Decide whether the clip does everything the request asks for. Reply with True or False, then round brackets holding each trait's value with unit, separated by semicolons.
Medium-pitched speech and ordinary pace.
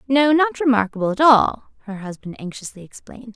False (235 Hz; 160 wpm)